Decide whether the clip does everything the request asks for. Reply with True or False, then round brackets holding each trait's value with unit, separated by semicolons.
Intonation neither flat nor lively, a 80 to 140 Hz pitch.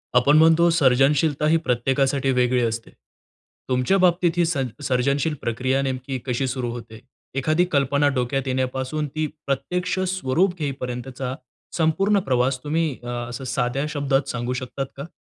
True (3.6 semitones; 135 Hz)